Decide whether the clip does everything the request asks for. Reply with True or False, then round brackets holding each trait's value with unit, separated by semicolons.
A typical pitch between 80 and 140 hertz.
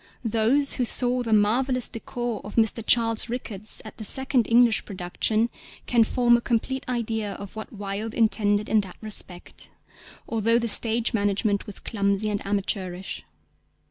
False (220 Hz)